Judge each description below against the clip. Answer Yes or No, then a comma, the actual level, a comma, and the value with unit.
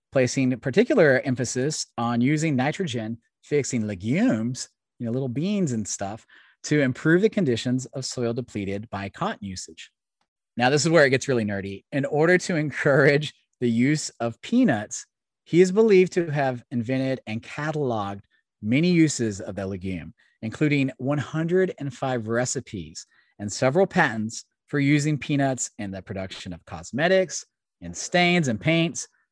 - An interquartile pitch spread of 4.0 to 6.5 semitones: Yes, average, 5.1 semitones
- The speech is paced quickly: No, average, 145 wpm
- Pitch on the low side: Yes, low, 130 Hz